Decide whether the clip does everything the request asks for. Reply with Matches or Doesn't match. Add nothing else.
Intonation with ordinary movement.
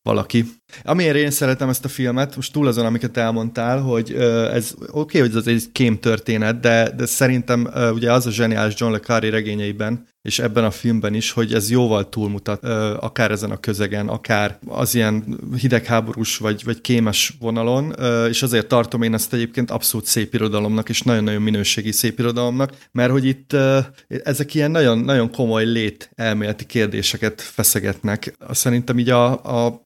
Doesn't match